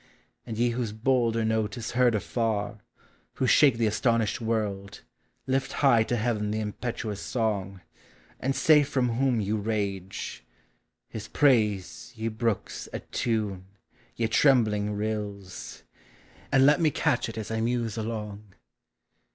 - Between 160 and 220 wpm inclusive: No, slow, 135 wpm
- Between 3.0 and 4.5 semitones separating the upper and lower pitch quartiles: No, narrow, 2.6 semitones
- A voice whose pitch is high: No, low, 110 Hz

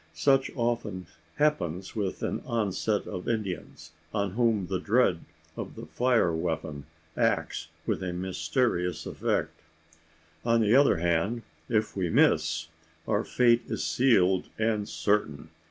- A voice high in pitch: No, low, 100 Hz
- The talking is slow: Yes, slow, 130 wpm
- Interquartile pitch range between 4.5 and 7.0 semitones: Yes, average, 4.9 semitones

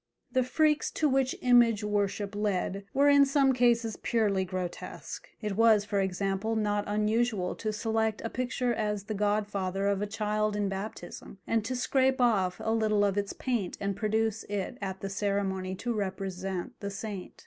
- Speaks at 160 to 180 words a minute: Yes, average, 170 wpm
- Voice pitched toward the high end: Yes, high, 210 Hz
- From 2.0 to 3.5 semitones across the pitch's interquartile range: Yes, narrow, 2.5 semitones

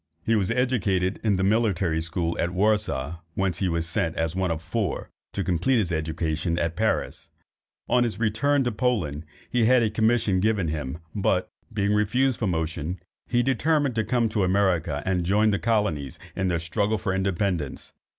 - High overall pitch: No, very low, 95 Hz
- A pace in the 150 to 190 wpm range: Yes, average, 175 wpm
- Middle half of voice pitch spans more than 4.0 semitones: Yes, average, 4.8 semitones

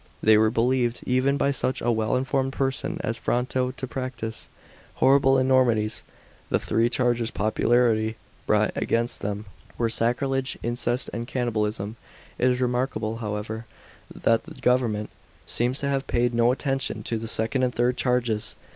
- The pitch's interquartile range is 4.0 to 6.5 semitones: No, narrow, 2.5 semitones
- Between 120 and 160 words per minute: Yes, average, 150 wpm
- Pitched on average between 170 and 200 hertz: No, low, 120 Hz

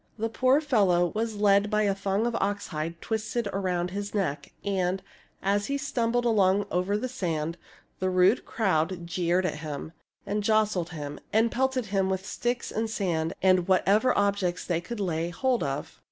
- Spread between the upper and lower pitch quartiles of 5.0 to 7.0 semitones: No, average, 3.7 semitones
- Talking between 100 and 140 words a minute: No, average, 170 wpm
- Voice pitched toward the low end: No, high, 195 Hz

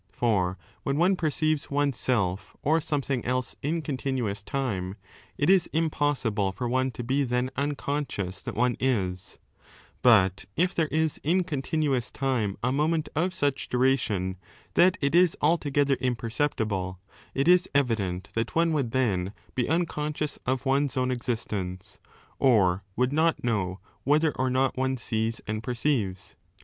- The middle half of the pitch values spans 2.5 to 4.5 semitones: No, average, 5.1 semitones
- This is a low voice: Yes, low, 130 Hz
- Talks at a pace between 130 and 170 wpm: Yes, average, 150 wpm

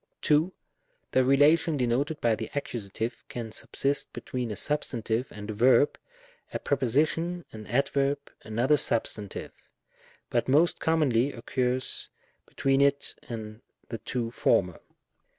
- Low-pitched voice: Yes, low, 130 Hz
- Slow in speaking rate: Yes, slow, 125 wpm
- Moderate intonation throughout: Yes, average, 4.0 semitones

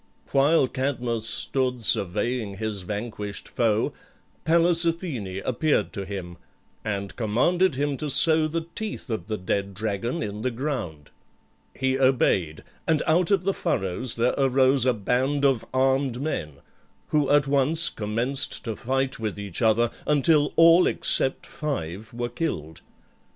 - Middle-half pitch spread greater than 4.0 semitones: Yes, wide, 5.6 semitones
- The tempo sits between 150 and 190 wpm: No, average, 140 wpm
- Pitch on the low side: Yes, low, 125 Hz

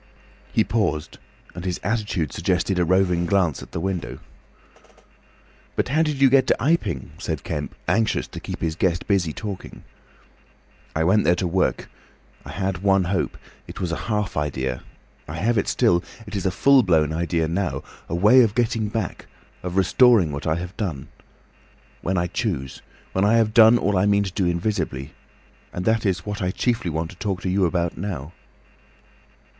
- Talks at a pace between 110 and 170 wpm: No, average, 180 wpm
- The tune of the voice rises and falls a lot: No, average, 3.7 semitones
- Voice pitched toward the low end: Yes, very low, 95 Hz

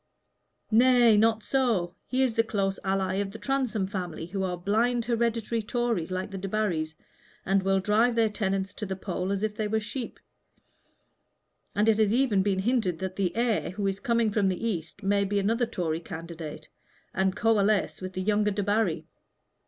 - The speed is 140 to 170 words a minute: No, average, 180 wpm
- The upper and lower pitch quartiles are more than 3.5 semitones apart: No, average, 3.0 semitones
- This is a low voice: No, high, 205 Hz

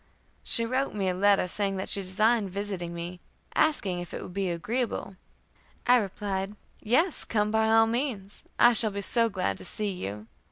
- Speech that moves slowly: No, average, 185 wpm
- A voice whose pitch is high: Yes, high, 205 Hz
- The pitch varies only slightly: No, average, 3.3 semitones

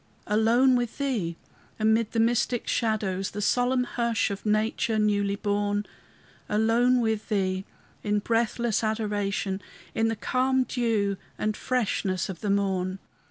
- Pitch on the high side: Yes, high, 215 Hz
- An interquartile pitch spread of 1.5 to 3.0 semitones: Yes, average, 2.7 semitones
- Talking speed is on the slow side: Yes, slow, 130 wpm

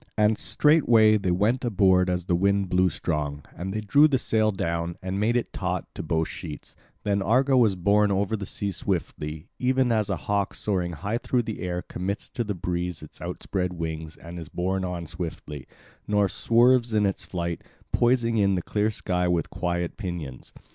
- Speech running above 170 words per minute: Yes, average, 190 wpm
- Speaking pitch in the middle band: No, very low, 95 Hz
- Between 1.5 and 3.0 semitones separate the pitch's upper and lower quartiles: No, average, 3.7 semitones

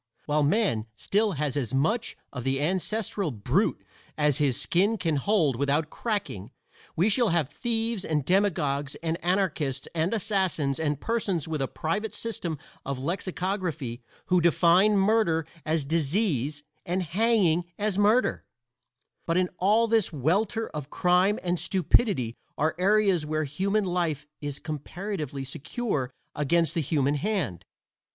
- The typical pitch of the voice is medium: Yes, medium, 170 Hz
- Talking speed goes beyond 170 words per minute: No, average, 140 wpm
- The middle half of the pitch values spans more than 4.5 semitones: Yes, wide, 5.6 semitones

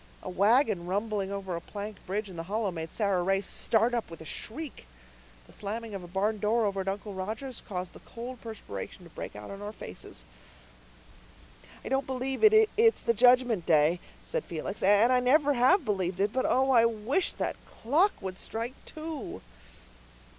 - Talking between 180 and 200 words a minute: Yes, average, 185 wpm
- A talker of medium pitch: No, high, 215 Hz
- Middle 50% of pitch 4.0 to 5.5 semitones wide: Yes, average, 4.6 semitones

